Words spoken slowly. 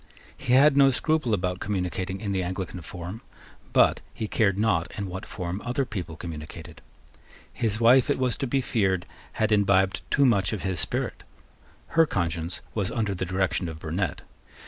No: average, 170 wpm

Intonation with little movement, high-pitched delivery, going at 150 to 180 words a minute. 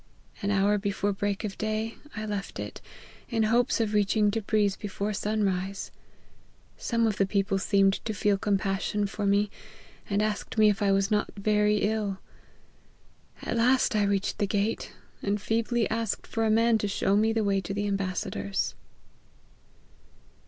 Yes: narrow, 1.5 semitones; high, 205 Hz; average, 165 wpm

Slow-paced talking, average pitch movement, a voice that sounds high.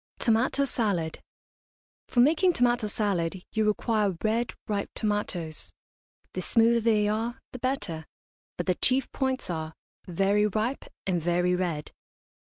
Yes: slow, 130 wpm; average, 4.8 semitones; high, 210 Hz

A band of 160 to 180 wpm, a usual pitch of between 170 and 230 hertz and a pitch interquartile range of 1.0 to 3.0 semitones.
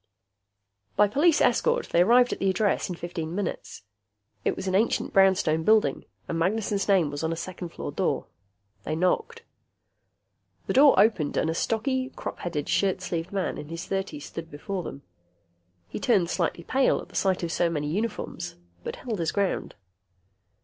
No: average, 170 wpm; medium, 185 Hz; average, 4.5 semitones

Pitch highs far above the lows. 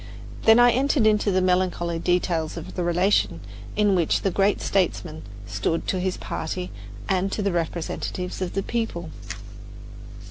No: average, 2.7 semitones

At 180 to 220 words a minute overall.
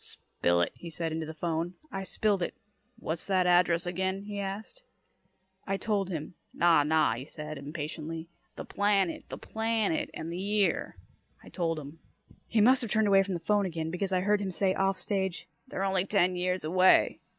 Yes: average, 190 wpm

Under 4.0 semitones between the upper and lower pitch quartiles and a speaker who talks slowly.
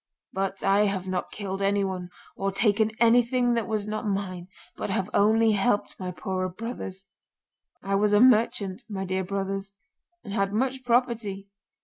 No: narrow, 2.5 semitones; average, 155 wpm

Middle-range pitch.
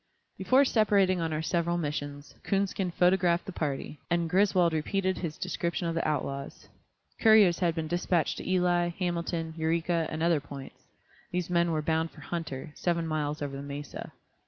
Yes: medium, 170 Hz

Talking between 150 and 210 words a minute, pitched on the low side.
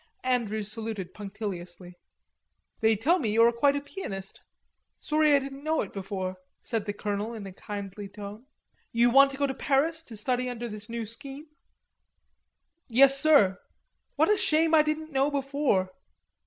No: average, 165 wpm; high, 235 Hz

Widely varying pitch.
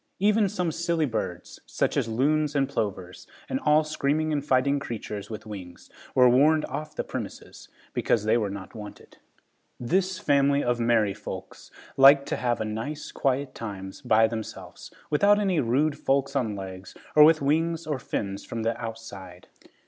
Yes: wide, 5.9 semitones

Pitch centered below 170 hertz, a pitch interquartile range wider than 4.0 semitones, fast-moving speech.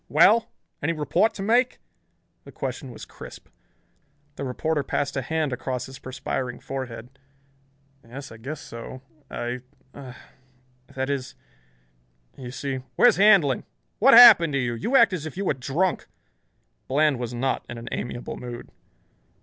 No: low, 135 Hz; average, 4.4 semitones; average, 150 wpm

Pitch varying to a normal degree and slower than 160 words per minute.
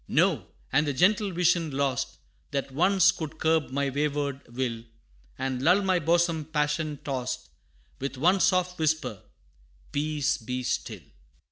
Yes: average, 4.1 semitones; slow, 135 wpm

